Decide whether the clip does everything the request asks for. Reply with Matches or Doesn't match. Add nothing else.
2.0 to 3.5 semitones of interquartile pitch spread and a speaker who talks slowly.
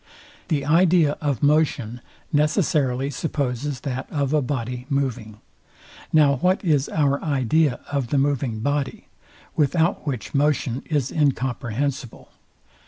Matches